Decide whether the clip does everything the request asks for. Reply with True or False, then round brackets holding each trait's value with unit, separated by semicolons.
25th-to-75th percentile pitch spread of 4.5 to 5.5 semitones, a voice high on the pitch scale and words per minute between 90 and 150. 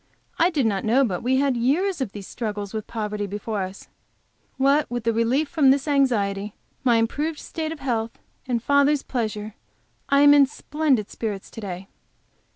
False (5.1 semitones; 240 Hz; 175 wpm)